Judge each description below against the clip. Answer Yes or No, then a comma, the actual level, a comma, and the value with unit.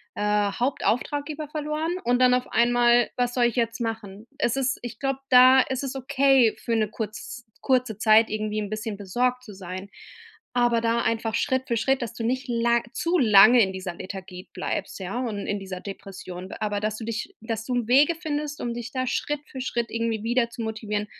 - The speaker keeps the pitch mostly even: No, average, 3.1 semitones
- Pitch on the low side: No, high, 235 Hz